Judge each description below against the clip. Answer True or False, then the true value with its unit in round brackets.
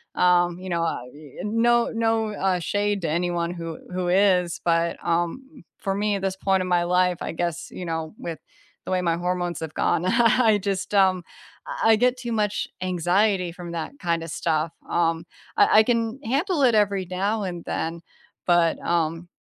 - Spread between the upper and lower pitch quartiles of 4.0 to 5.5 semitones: False (3.5 semitones)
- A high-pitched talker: False (180 Hz)